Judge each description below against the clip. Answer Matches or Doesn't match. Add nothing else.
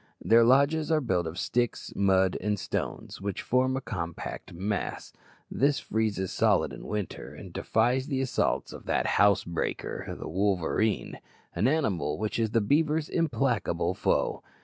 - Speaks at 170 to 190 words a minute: Doesn't match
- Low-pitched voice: Matches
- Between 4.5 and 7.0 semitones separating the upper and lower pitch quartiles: Matches